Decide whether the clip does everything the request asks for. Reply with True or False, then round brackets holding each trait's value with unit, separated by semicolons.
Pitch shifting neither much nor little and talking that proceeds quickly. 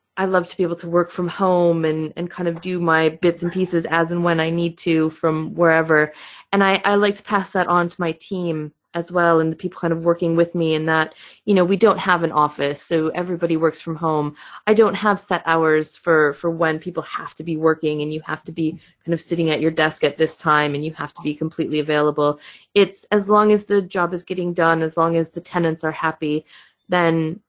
False (2.0 semitones; 245 wpm)